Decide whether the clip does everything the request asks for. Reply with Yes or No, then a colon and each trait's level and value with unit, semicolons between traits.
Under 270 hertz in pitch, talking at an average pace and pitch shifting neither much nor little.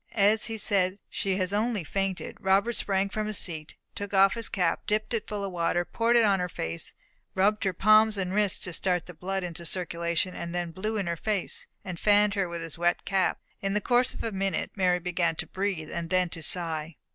No: high, 190 Hz; fast, 220 wpm; average, 3.0 semitones